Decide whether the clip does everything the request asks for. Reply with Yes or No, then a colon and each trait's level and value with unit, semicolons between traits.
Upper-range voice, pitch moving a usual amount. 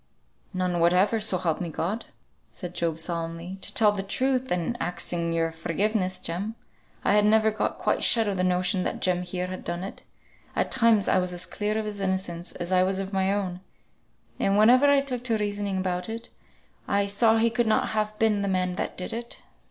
Yes: high, 195 Hz; average, 3.3 semitones